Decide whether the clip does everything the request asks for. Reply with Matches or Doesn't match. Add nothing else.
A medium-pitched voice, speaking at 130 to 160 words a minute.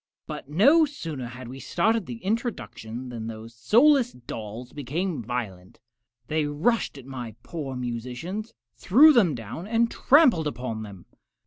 Matches